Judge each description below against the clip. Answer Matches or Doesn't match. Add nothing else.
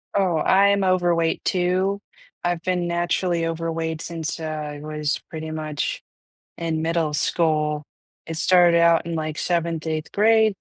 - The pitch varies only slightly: Matches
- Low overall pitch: Doesn't match